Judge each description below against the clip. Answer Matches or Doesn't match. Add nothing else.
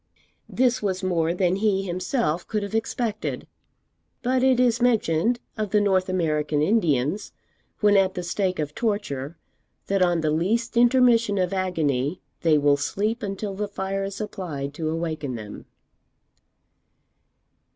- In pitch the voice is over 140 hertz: Matches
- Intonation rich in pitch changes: Doesn't match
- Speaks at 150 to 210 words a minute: Doesn't match